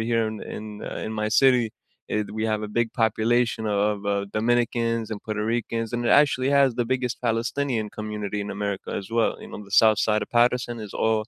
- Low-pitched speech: Yes, low, 115 Hz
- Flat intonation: Yes, narrow, 2.1 semitones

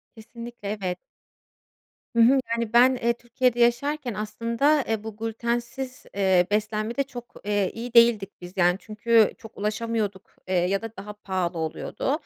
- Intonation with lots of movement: No, average, 2.7 semitones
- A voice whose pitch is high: Yes, high, 225 Hz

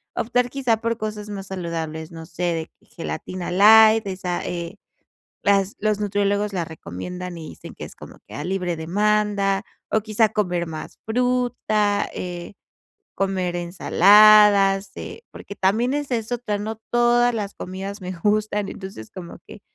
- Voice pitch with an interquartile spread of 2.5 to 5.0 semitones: Yes, average, 3.2 semitones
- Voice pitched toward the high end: Yes, high, 200 Hz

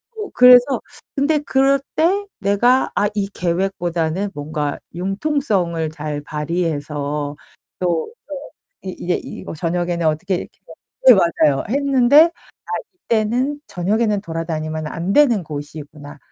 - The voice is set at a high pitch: No, medium, 180 Hz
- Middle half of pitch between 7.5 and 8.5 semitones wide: Yes, wide, 7.9 semitones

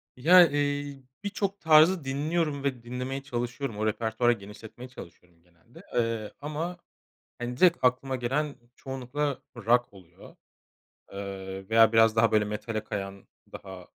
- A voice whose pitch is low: Yes, low, 120 Hz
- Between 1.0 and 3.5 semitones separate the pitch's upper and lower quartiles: No, average, 4.8 semitones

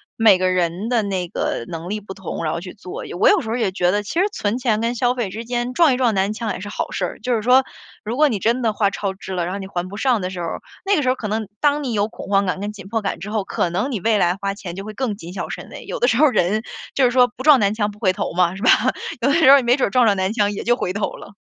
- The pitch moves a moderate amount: Yes, average, 4.2 semitones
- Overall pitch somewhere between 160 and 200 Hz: No, high, 210 Hz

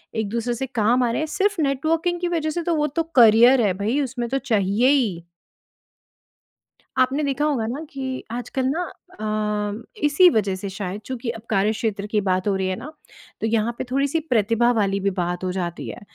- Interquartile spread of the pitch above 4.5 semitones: Yes, average, 5.1 semitones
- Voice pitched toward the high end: Yes, high, 240 Hz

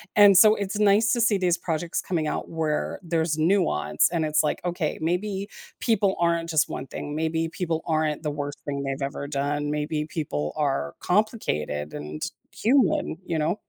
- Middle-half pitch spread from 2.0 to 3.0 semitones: No, average, 4.2 semitones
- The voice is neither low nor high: Yes, medium, 160 Hz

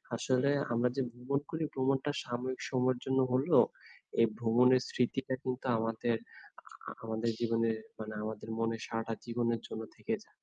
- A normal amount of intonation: No, narrow, 2.2 semitones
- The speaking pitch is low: Yes, low, 120 Hz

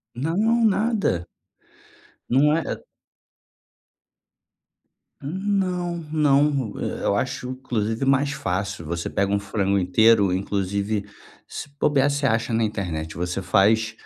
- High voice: No, low, 115 Hz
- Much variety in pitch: Yes, wide, 6.8 semitones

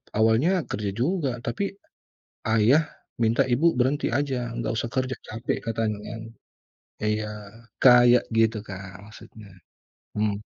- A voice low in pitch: Yes, low, 115 Hz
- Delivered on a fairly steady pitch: No, average, 3.4 semitones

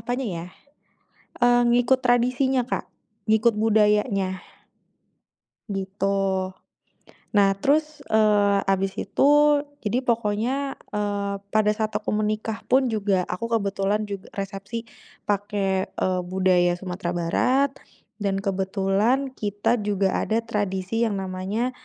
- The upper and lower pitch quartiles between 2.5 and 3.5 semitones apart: Yes, average, 2.9 semitones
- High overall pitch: Yes, high, 205 Hz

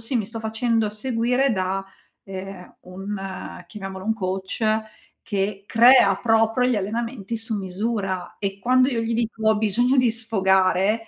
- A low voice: No, high, 215 Hz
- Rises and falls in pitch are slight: No, average, 3.1 semitones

